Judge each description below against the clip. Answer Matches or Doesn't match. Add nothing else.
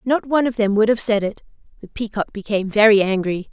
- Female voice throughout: Matches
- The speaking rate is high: Matches